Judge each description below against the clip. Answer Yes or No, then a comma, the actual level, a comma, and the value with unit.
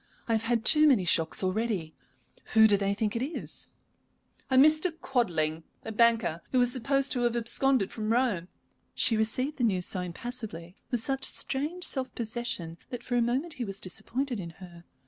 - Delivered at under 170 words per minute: No, average, 185 wpm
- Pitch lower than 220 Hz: No, high, 230 Hz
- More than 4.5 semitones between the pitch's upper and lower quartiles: Yes, average, 5.2 semitones